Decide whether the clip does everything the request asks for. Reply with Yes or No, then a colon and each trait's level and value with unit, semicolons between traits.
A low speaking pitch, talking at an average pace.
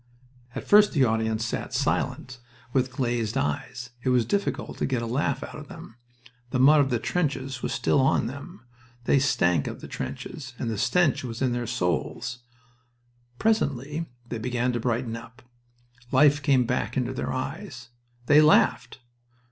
Yes: low, 125 Hz; average, 165 wpm